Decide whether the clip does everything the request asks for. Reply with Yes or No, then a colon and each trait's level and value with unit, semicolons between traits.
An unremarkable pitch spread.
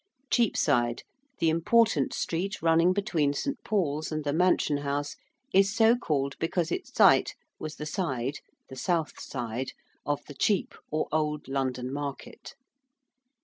Yes: average, 4.3 semitones